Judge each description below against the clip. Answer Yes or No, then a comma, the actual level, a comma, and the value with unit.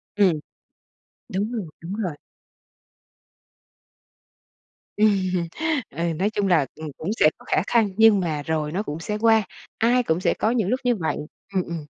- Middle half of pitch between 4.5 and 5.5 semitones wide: Yes, average, 4.9 semitones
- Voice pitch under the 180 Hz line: No, high, 190 Hz